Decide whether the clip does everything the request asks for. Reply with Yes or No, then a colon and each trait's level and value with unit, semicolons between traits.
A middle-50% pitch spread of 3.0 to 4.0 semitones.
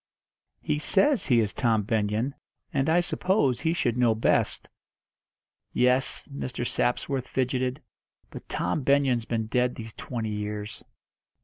Yes: average, 3.7 semitones